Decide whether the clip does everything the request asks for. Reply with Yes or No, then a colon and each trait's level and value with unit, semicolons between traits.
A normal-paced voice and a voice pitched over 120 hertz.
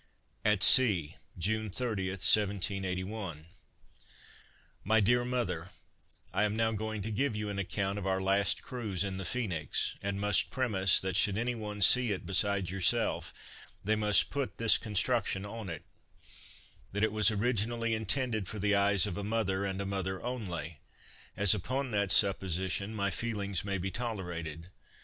No: average, 160 wpm; low, 100 Hz